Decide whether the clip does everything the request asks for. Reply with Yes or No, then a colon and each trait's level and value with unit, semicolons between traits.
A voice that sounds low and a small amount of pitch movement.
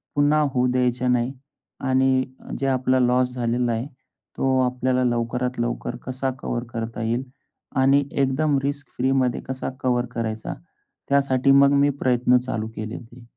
Yes: low, 125 Hz; narrow, 1.7 semitones